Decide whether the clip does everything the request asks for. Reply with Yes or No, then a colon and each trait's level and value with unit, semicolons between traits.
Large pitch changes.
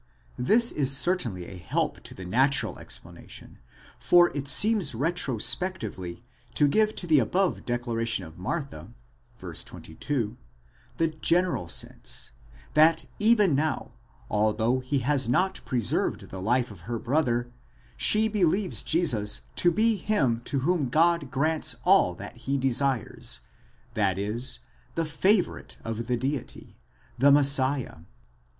Yes: wide, 6.6 semitones